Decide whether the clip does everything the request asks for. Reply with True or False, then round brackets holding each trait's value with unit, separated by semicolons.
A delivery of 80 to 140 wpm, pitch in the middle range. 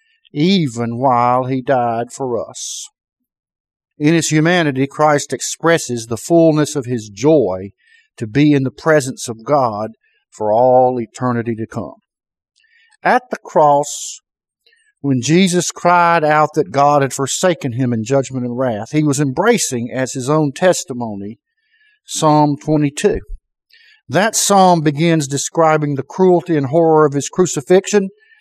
True (135 wpm; 150 Hz)